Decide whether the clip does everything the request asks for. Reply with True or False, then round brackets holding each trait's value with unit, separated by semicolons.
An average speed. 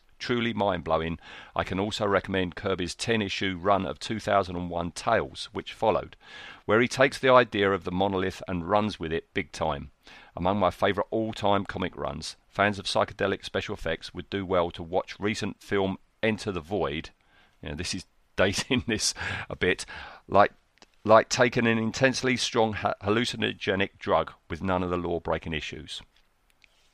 True (170 wpm)